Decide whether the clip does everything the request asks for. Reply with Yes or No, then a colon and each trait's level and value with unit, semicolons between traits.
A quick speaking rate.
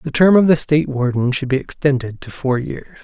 Yes: fast, 240 wpm